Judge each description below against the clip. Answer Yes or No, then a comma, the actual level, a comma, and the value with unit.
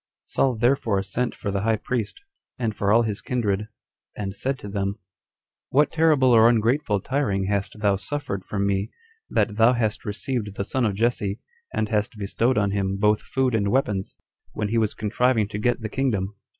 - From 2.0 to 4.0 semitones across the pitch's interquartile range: Yes, average, 3.5 semitones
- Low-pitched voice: Yes, low, 110 Hz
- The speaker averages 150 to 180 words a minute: No, average, 190 wpm